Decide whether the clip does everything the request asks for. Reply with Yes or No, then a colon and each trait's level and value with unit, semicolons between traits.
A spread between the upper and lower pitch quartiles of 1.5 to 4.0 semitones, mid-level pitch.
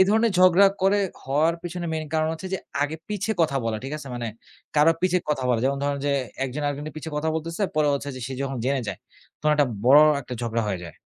Yes: average, 3.7 semitones; medium, 150 Hz